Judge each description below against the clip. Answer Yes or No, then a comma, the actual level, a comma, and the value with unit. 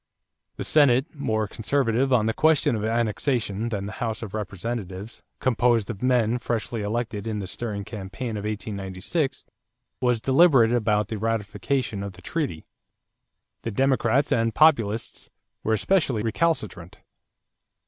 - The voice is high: No, low, 115 Hz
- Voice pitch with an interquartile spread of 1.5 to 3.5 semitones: Yes, average, 3.2 semitones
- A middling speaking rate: No, slow, 130 wpm